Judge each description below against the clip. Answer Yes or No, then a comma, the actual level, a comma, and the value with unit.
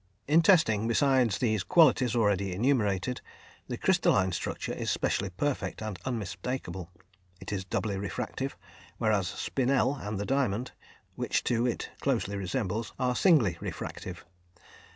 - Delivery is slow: Yes, slow, 130 wpm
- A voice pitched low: Yes, low, 110 Hz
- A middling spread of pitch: Yes, average, 4.8 semitones